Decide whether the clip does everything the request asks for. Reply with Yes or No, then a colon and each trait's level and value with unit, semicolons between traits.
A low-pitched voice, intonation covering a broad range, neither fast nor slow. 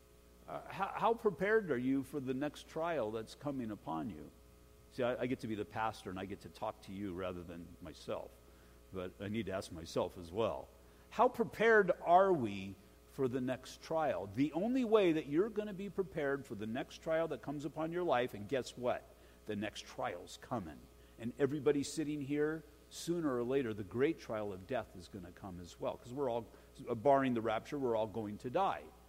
No: low, 120 Hz; wide, 7.7 semitones; fast, 210 wpm